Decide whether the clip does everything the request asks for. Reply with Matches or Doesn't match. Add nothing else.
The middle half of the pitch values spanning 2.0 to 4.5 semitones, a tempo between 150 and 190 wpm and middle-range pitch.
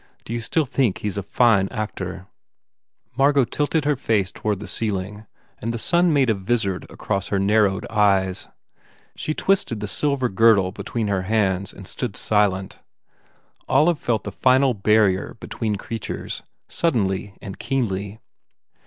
Doesn't match